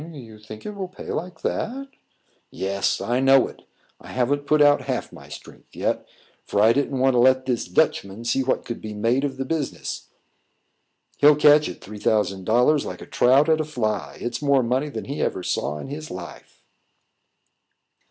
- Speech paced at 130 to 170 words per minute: No, average, 190 wpm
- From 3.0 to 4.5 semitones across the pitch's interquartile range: No, average, 4.9 semitones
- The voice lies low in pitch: Yes, low, 130 Hz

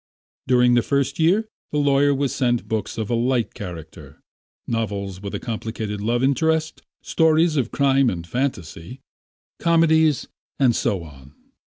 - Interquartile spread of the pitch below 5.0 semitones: No, wide, 5.4 semitones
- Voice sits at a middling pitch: No, low, 125 Hz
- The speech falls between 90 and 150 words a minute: Yes, average, 145 wpm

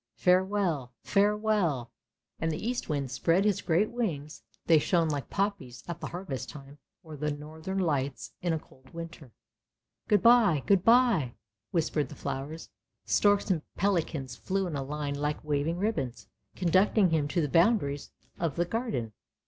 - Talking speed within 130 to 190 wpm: Yes, average, 155 wpm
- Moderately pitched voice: Yes, medium, 165 Hz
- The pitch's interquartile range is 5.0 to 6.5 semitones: Yes, average, 5.3 semitones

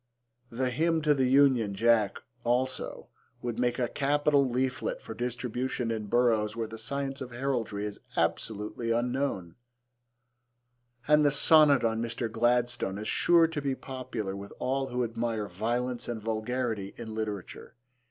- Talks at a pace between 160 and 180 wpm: No, average, 145 wpm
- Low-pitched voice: Yes, low, 120 Hz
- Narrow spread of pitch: No, average, 3.1 semitones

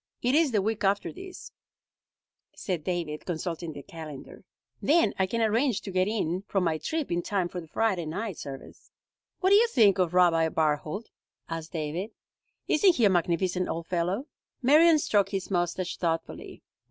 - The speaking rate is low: No, average, 170 wpm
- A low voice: No, medium, 185 Hz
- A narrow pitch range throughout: No, average, 5.2 semitones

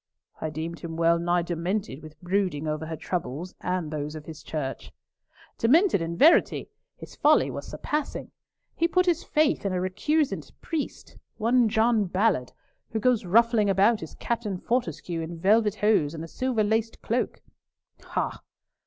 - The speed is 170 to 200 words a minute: No, average, 155 wpm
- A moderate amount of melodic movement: No, wide, 5.9 semitones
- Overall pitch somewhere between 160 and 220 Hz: Yes, high, 190 Hz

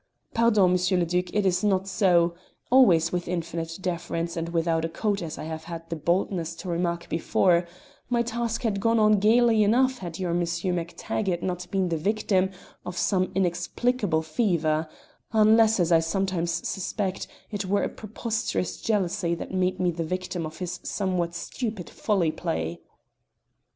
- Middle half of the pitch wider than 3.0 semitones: Yes, average, 3.5 semitones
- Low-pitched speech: No, medium, 180 Hz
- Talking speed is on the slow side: No, average, 165 wpm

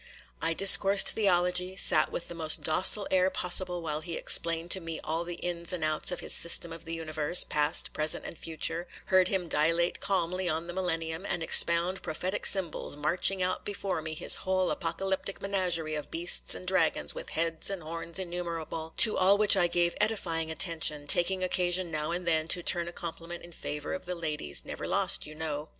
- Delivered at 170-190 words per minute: Yes, average, 185 wpm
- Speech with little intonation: Yes, narrow, 2.2 semitones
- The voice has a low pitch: No, medium, 170 Hz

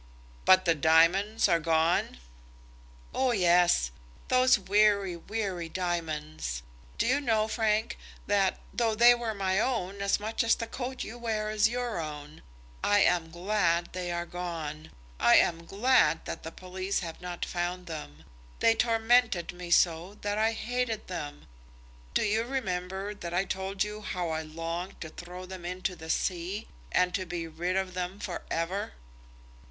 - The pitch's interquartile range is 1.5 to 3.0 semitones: No, average, 4.0 semitones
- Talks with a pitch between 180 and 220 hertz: Yes, medium, 185 Hz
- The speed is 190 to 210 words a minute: No, average, 160 wpm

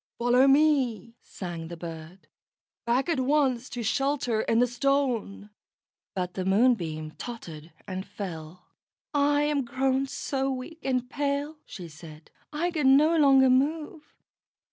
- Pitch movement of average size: No, wide, 6.9 semitones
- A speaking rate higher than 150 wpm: No, slow, 135 wpm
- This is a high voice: Yes, very high, 255 Hz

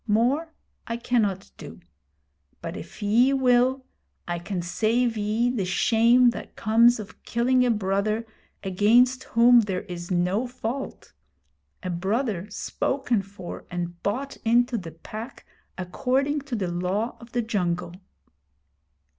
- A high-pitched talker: Yes, high, 225 Hz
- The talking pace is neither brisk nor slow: No, slow, 130 wpm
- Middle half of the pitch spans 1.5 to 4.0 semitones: No, average, 4.4 semitones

